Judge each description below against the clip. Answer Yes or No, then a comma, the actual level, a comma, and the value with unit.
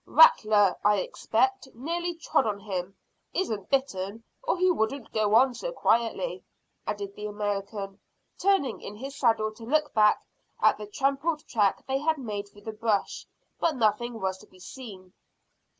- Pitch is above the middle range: Yes, high, 225 Hz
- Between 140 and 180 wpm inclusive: Yes, average, 160 wpm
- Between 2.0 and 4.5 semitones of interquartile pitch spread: No, average, 5.2 semitones